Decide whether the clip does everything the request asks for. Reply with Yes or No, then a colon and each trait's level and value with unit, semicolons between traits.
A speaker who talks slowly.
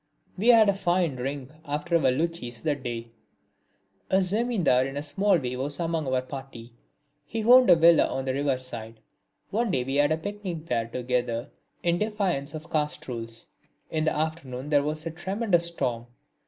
No: average, 180 wpm